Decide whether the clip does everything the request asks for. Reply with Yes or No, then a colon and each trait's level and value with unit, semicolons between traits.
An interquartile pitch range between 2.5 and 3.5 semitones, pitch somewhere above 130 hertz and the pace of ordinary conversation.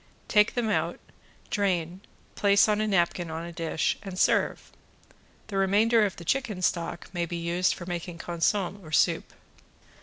Yes: average, 3.2 semitones; medium, 185 Hz; average, 160 wpm